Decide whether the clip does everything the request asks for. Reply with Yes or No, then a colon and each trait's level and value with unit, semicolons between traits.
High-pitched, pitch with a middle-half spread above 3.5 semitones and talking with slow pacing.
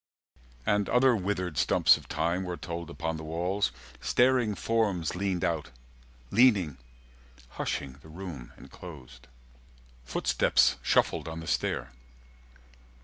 No: very low, 85 Hz; average, 4.5 semitones; slow, 115 wpm